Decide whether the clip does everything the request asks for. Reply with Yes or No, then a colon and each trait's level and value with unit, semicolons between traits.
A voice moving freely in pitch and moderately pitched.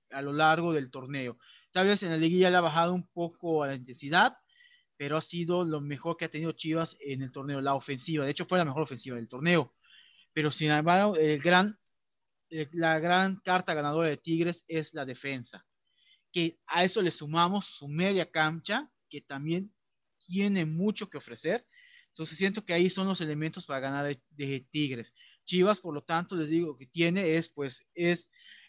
No: average, 3.7 semitones; medium, 165 Hz